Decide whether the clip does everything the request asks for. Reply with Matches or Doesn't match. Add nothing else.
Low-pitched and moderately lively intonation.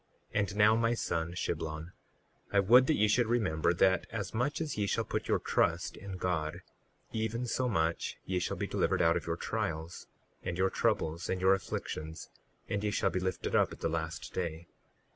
Matches